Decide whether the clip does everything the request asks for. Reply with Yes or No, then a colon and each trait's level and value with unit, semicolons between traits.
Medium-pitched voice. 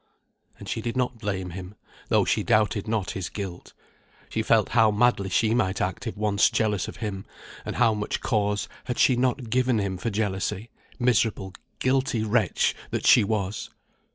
No: low, 105 Hz